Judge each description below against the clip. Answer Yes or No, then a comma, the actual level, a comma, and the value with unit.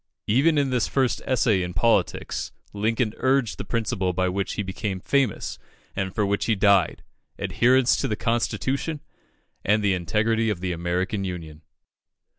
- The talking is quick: No, average, 155 wpm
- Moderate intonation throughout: Yes, average, 4.2 semitones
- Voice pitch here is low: Yes, low, 105 Hz